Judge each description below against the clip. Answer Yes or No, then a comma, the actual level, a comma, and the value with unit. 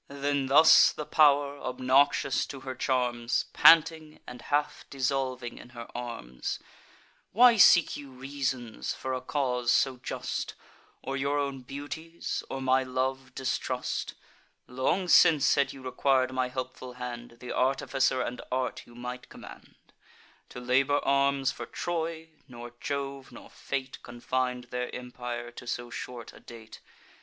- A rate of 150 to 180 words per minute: No, average, 140 wpm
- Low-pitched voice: Yes, low, 130 Hz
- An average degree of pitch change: No, narrow, 2.1 semitones